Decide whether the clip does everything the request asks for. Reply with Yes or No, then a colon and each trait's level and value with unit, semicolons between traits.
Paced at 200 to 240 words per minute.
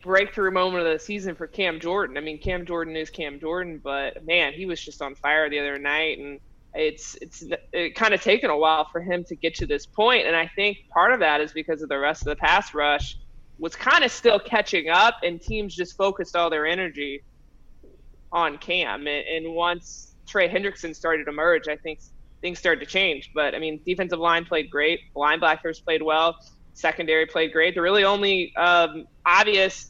Yes: fast, 205 wpm